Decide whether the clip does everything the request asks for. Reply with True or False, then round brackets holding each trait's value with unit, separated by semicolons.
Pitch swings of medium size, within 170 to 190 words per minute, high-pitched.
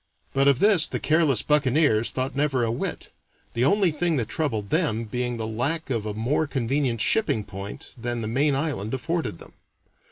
False (4.9 semitones; 185 wpm; 130 Hz)